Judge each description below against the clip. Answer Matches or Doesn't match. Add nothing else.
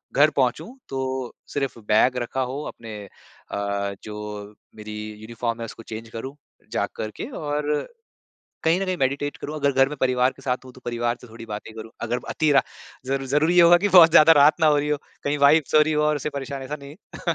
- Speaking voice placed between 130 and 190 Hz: Matches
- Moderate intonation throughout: Matches